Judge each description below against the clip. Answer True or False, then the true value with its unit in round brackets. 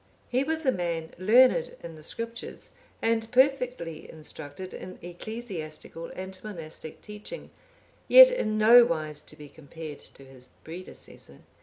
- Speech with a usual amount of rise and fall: False (7.0 semitones)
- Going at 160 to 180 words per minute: False (140 wpm)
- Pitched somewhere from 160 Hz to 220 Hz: True (185 Hz)